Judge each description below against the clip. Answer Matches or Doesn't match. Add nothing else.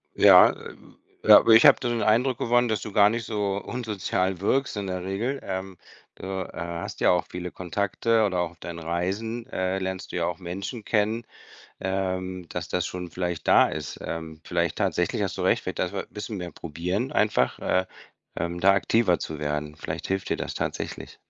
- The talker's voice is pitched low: Matches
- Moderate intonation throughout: Matches